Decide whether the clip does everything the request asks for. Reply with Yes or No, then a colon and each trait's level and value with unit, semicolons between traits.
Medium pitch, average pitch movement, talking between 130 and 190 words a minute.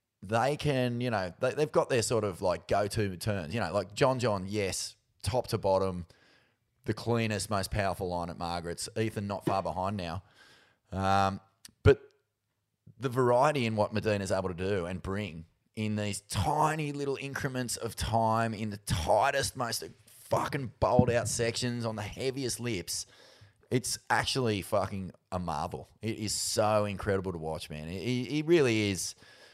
No: low, 105 Hz; average, 3.4 semitones; average, 165 wpm